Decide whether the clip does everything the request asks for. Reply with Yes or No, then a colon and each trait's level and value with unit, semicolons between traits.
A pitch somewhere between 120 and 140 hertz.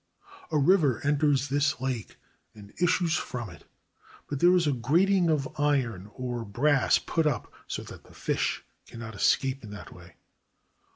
Yes: low, 135 Hz